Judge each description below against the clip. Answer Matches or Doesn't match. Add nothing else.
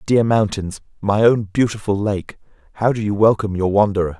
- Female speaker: Doesn't match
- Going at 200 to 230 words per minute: Doesn't match